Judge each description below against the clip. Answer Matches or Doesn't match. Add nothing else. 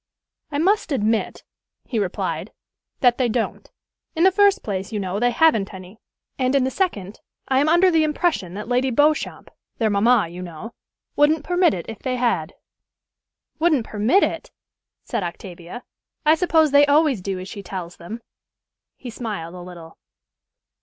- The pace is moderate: Matches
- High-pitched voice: Matches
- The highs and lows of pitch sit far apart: Matches